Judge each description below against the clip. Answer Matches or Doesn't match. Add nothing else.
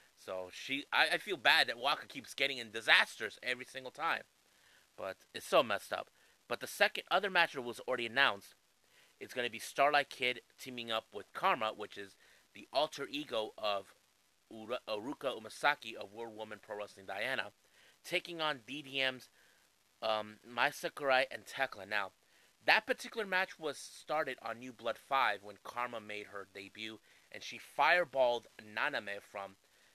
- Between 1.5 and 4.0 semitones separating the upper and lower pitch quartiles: Doesn't match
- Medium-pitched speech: Doesn't match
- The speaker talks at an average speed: Matches